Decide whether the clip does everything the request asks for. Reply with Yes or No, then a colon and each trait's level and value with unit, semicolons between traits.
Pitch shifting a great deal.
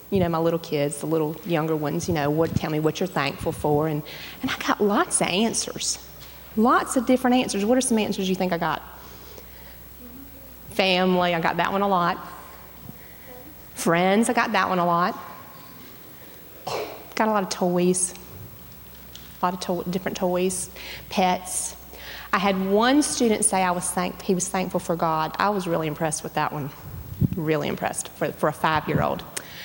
No: average, 3.9 semitones